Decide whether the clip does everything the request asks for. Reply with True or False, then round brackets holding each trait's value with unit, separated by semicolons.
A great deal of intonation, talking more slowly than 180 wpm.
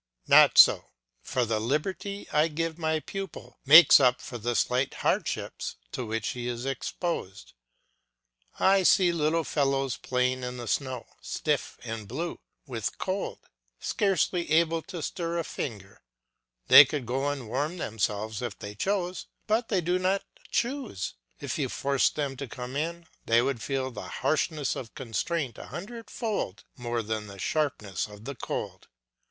True (6.1 semitones; 155 wpm)